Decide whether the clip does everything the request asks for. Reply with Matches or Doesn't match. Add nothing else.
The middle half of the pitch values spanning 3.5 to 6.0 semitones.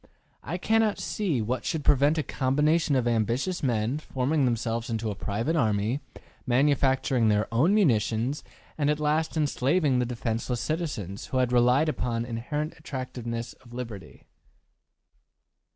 Matches